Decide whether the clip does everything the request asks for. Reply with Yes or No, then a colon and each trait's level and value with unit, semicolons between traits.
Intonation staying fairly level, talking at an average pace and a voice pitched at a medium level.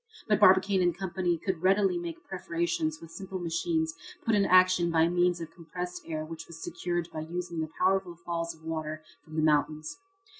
Yes: narrow, 2.3 semitones; average, 185 wpm; medium, 170 Hz